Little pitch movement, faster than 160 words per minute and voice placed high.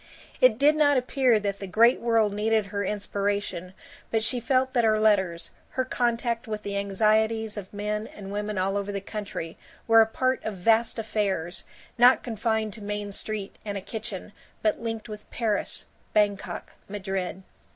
Yes: narrow, 2.2 semitones; average, 170 wpm; high, 215 Hz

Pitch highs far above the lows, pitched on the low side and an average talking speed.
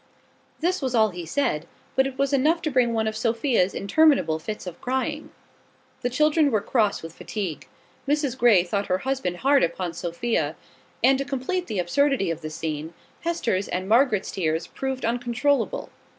No: wide, 7.1 semitones; high, 235 Hz; average, 175 wpm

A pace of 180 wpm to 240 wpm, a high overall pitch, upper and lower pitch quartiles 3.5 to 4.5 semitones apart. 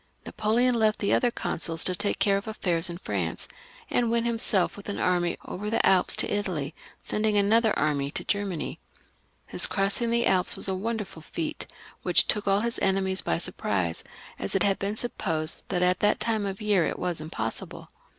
Yes: average, 190 wpm; high, 195 Hz; average, 3.9 semitones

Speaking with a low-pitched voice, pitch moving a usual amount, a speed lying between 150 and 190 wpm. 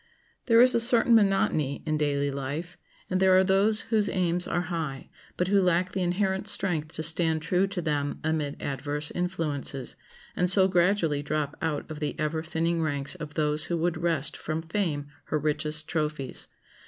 No: medium, 165 Hz; average, 3.6 semitones; average, 180 wpm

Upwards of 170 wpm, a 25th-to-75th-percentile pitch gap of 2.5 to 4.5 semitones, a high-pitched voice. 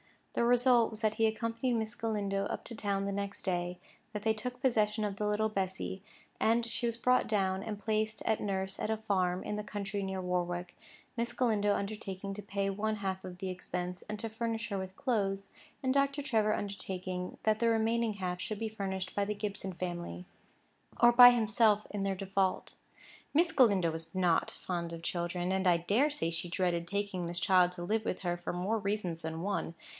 Yes: average, 200 wpm; average, 3.1 semitones; high, 200 Hz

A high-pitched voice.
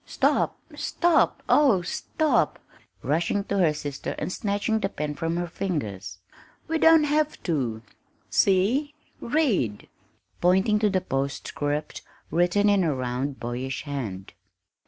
No: medium, 175 Hz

